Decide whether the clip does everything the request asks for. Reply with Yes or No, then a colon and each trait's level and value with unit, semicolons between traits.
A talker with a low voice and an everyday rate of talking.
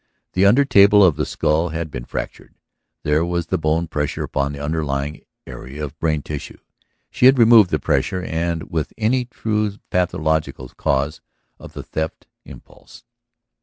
Yes: very low, 80 Hz; average, 165 wpm